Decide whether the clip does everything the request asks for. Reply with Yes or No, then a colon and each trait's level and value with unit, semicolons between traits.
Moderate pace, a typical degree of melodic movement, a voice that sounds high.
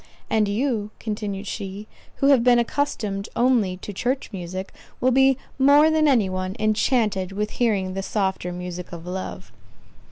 Yes: average, 155 wpm; average, 4.6 semitones; high, 210 Hz